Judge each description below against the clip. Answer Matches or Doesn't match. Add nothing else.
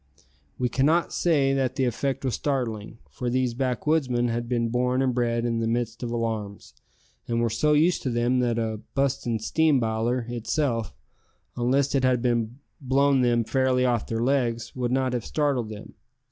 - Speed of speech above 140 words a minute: Matches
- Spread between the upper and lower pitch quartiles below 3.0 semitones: Matches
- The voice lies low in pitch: Matches